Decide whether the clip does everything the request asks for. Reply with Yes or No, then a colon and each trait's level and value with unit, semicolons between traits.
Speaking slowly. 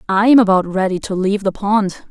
No: average, 200 wpm